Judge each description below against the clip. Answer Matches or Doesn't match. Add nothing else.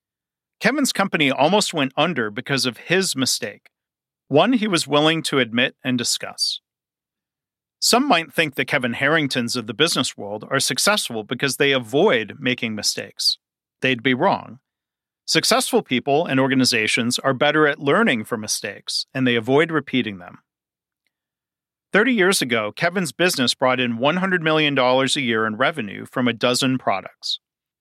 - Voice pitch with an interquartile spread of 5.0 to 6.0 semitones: Doesn't match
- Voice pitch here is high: Doesn't match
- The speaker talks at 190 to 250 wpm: Doesn't match